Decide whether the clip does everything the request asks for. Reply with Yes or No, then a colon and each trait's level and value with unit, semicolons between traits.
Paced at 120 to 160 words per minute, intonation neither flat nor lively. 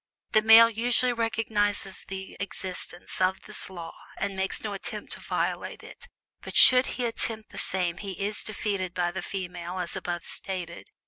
No: average, 170 wpm; average, 3.2 semitones